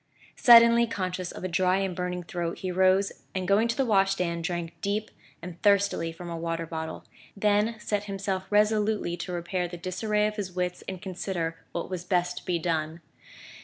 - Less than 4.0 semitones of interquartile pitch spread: Yes, average, 2.9 semitones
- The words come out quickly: No, average, 185 wpm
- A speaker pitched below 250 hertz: Yes, medium, 185 Hz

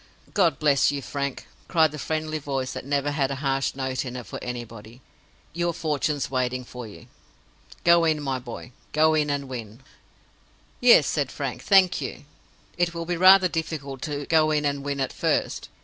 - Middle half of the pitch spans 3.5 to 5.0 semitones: No, average, 3.1 semitones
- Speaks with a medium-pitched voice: Yes, medium, 145 Hz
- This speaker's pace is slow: No, average, 180 wpm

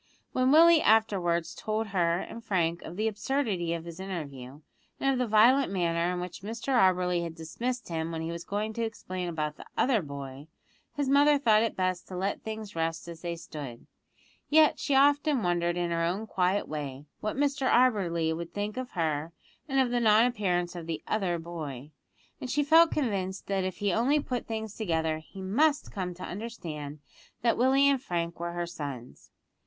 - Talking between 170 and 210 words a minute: Yes, average, 190 wpm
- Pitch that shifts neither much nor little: No, wide, 5.7 semitones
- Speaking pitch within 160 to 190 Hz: Yes, medium, 185 Hz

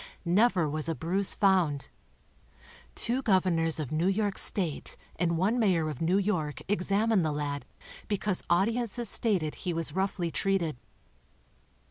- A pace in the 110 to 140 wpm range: Yes, slow, 135 wpm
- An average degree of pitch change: Yes, average, 3.8 semitones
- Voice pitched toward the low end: No, medium, 180 Hz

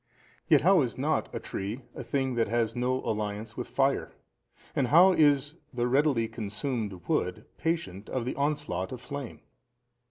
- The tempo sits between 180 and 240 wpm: No, average, 160 wpm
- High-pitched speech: No, low, 130 Hz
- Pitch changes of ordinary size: Yes, average, 4.4 semitones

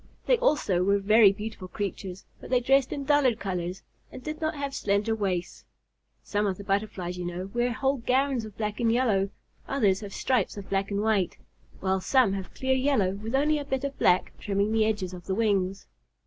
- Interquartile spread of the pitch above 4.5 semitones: Yes, average, 5.0 semitones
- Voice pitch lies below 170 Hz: No, high, 210 Hz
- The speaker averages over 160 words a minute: Yes, fast, 205 wpm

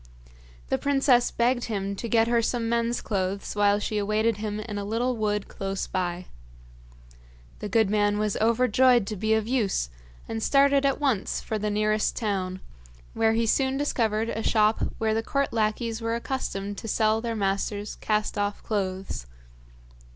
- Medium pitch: No, high, 220 Hz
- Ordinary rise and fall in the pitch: No, narrow, 2.2 semitones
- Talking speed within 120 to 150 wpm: No, average, 165 wpm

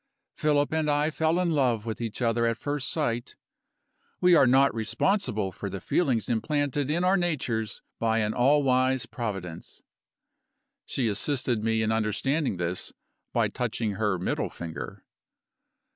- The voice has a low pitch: Yes, low, 120 Hz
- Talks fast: No, average, 145 wpm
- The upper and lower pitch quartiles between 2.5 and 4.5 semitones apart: No, average, 4.9 semitones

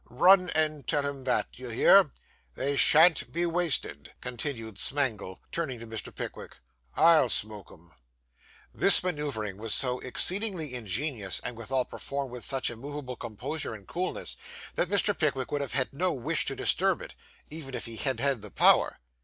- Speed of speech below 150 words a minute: No, average, 165 wpm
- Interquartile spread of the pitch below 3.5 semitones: No, average, 5.1 semitones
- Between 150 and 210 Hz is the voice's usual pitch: No, low, 135 Hz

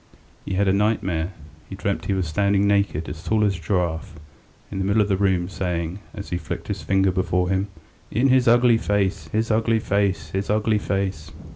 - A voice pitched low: Yes, very low, 95 Hz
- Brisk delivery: Yes, fast, 210 wpm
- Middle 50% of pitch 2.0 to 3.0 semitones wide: Yes, narrow, 2.5 semitones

